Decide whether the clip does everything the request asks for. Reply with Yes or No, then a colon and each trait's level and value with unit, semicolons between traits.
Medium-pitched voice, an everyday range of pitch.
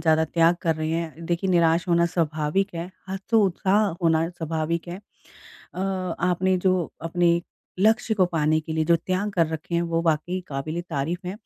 No: medium, 170 Hz; narrow, 2.2 semitones